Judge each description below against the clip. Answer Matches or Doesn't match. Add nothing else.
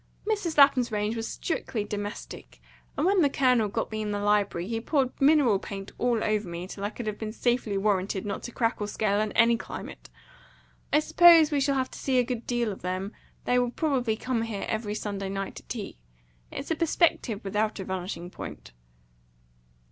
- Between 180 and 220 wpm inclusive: Matches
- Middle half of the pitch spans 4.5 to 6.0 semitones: Doesn't match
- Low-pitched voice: Doesn't match